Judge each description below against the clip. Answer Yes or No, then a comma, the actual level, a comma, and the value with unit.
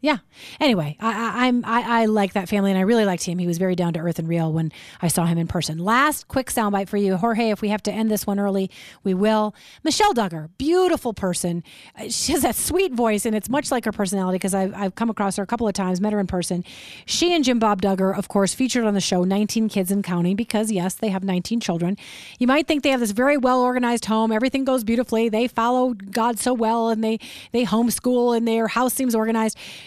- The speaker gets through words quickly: Yes, fast, 245 wpm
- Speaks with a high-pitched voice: Yes, high, 220 Hz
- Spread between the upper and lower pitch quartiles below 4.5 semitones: Yes, average, 3.8 semitones